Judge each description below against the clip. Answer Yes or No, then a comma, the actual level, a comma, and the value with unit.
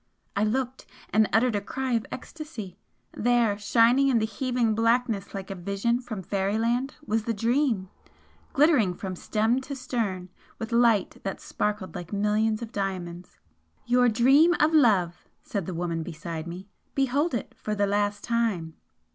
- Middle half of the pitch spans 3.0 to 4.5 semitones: Yes, average, 3.9 semitones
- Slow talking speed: No, average, 155 wpm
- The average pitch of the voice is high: Yes, high, 220 Hz